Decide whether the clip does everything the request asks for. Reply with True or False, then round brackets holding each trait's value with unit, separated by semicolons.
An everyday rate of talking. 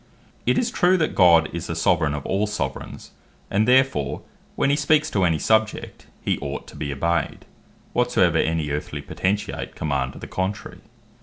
True (170 wpm)